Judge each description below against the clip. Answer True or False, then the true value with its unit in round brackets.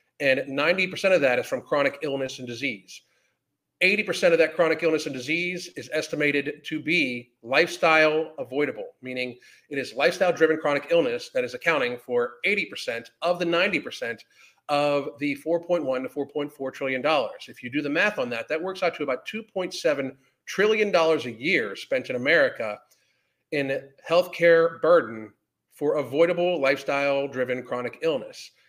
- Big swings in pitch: False (4.2 semitones)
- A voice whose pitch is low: False (155 Hz)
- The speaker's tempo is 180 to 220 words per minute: False (155 wpm)